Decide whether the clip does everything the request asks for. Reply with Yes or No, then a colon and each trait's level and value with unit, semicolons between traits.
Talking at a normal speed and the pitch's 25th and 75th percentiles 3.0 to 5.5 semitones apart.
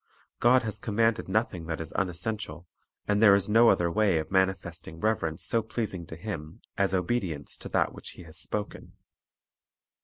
Yes: average, 175 wpm; average, 4.5 semitones